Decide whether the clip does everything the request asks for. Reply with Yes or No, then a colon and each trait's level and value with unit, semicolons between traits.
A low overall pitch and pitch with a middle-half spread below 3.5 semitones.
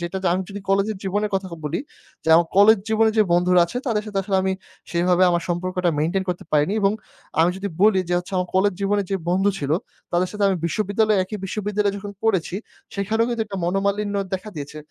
No: high, 195 Hz; narrow, 2.5 semitones